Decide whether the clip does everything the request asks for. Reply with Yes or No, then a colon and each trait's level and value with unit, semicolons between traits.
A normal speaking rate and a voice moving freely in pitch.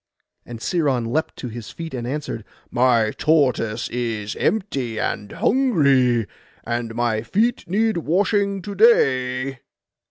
No: slow, 120 wpm; wide, 6.9 semitones